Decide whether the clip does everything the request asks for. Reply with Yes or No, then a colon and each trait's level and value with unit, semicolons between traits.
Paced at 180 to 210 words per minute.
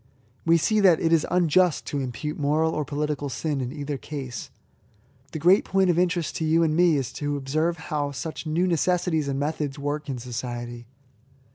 Yes: average, 185 wpm